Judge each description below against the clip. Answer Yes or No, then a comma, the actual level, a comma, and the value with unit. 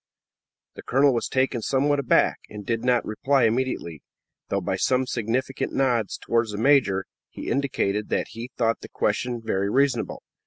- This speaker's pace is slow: No, average, 160 wpm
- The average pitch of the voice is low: Yes, low, 120 Hz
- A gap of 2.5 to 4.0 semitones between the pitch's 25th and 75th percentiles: Yes, average, 3.7 semitones